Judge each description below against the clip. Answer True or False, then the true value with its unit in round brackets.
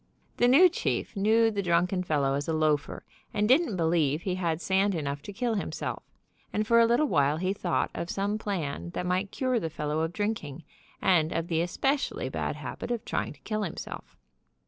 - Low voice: False (185 Hz)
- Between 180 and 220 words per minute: True (200 wpm)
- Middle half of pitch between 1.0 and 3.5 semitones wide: False (5.1 semitones)